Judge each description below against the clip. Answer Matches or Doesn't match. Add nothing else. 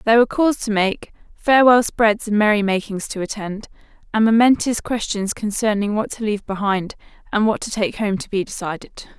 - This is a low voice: Doesn't match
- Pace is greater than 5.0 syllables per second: Matches